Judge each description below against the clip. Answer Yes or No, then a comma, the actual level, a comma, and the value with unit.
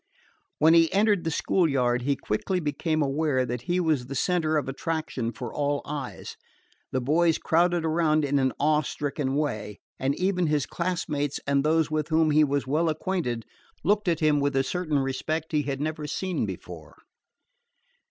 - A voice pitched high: No, medium, 150 Hz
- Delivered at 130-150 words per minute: No, average, 175 wpm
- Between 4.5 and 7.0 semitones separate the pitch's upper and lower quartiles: No, average, 3.0 semitones